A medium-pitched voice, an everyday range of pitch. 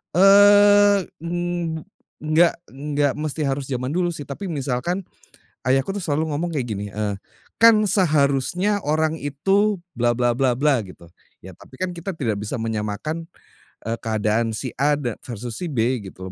No: medium, 145 Hz; wide, 6.4 semitones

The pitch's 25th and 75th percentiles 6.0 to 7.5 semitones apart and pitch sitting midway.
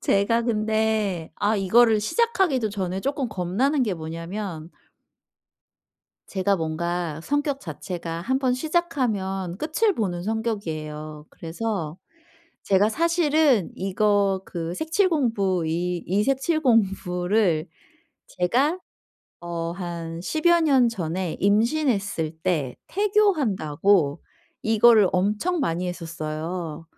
No: wide, 6.7 semitones; high, 200 Hz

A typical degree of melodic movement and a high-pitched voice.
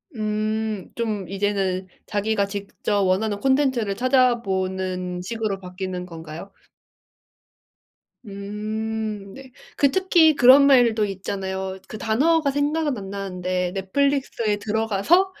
Yes: average, 4.3 semitones; high, 210 Hz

